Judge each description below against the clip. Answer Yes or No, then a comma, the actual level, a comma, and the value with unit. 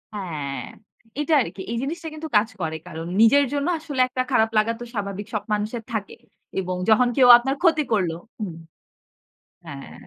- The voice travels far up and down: Yes, wide, 6.1 semitones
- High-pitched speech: Yes, high, 220 Hz